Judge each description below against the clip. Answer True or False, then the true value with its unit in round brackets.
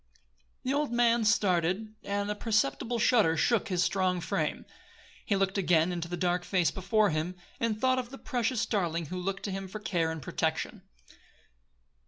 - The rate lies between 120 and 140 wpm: False (175 wpm)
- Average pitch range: True (4.1 semitones)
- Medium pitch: False (195 Hz)